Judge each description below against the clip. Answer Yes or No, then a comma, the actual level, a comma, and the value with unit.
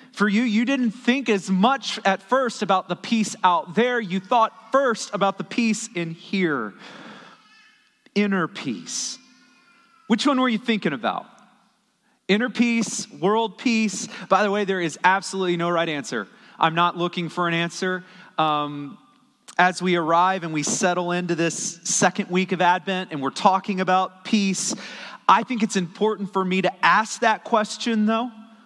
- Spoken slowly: No, average, 165 wpm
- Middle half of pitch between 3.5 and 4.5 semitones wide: Yes, average, 3.9 semitones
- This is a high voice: Yes, high, 200 Hz